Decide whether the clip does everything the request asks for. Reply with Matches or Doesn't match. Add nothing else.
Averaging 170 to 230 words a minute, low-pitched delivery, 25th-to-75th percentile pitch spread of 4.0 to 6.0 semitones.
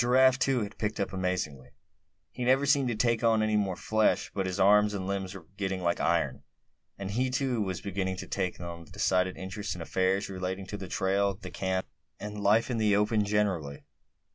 Doesn't match